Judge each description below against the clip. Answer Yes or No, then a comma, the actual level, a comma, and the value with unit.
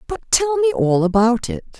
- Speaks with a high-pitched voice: Yes, high, 245 Hz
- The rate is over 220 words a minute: No, average, 200 wpm